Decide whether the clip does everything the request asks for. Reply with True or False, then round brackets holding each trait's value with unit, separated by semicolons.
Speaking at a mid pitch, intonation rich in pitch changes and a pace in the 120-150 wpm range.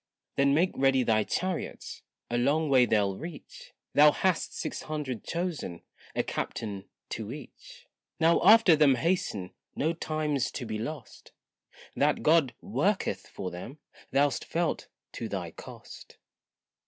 True (145 Hz; 6.4 semitones; 135 wpm)